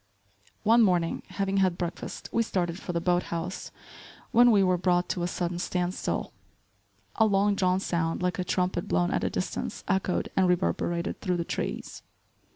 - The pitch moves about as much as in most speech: No, narrow, 1.8 semitones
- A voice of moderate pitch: Yes, medium, 180 Hz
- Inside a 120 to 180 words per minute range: Yes, average, 175 wpm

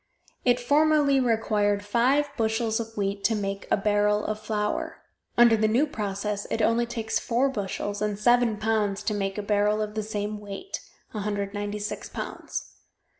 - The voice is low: No, high, 215 Hz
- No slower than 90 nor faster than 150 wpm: No, average, 160 wpm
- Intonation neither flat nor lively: No, narrow, 2.2 semitones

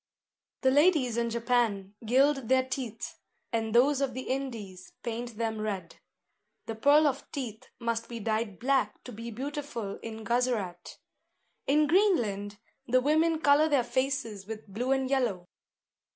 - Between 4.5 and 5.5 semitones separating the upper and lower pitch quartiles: No, average, 3.7 semitones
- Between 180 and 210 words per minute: No, average, 145 wpm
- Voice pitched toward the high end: Yes, high, 240 Hz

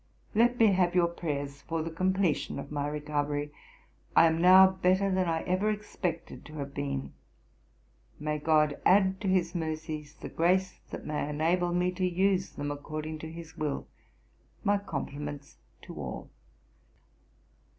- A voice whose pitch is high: No, medium, 165 Hz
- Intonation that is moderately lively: Yes, average, 3.8 semitones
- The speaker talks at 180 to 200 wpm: No, average, 150 wpm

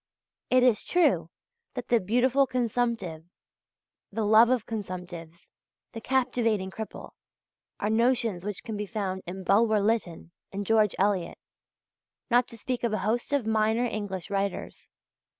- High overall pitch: Yes, high, 220 Hz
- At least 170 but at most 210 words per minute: No, average, 140 wpm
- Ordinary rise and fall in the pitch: Yes, average, 3.5 semitones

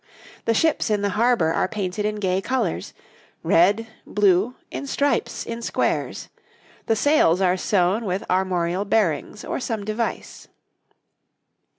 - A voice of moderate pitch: No, high, 205 Hz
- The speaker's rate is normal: No, slow, 130 wpm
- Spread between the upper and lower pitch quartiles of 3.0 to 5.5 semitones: Yes, average, 3.7 semitones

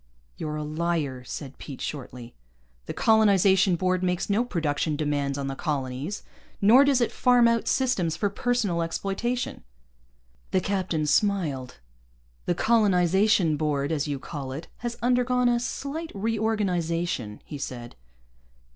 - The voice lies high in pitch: No, medium, 175 Hz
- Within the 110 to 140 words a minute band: Yes, slow, 135 wpm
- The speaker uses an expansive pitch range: Yes, wide, 6.8 semitones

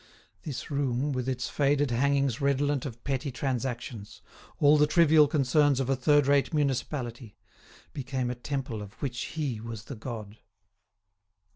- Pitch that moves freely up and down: No, average, 3.0 semitones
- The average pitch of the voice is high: No, low, 135 Hz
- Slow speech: No, average, 145 wpm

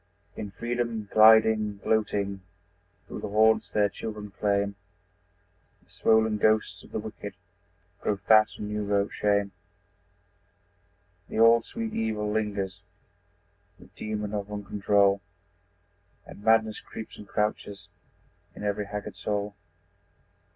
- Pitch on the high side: No, low, 105 Hz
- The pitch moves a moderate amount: No, narrow, 1.3 semitones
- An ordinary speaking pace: No, slow, 115 wpm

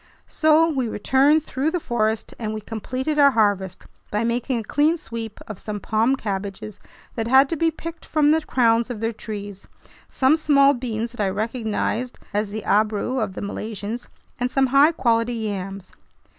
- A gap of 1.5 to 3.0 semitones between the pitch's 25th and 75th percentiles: No, average, 4.2 semitones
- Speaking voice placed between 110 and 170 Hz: No, high, 230 Hz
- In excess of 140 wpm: Yes, average, 175 wpm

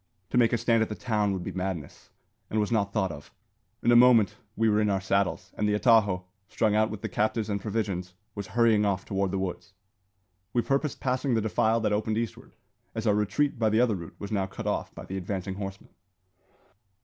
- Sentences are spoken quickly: Yes, fast, 220 wpm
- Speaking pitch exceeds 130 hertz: No, low, 105 Hz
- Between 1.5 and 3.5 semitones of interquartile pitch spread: Yes, average, 2.7 semitones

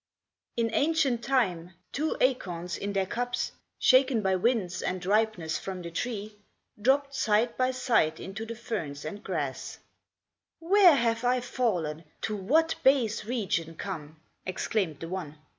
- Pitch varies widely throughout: Yes, wide, 5.8 semitones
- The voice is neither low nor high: No, high, 215 Hz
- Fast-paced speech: No, average, 140 wpm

